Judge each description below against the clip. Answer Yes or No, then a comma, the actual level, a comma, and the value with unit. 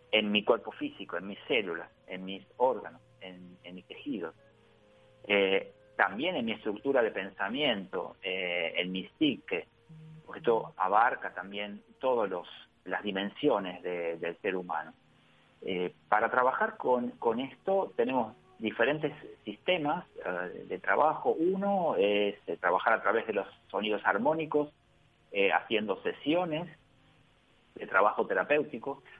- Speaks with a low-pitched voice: Yes, low, 115 Hz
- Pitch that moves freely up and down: Yes, wide, 7.8 semitones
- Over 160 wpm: No, slow, 125 wpm